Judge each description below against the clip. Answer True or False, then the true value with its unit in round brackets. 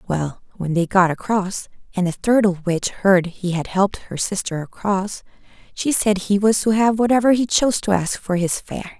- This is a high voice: True (195 Hz)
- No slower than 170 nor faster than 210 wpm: True (205 wpm)